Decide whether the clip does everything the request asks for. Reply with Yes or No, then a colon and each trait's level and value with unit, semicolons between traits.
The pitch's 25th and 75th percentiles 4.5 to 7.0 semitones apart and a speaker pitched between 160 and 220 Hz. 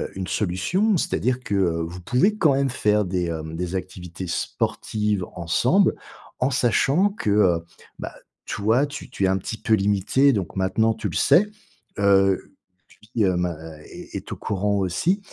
No: wide, 5.5 semitones; low, 100 Hz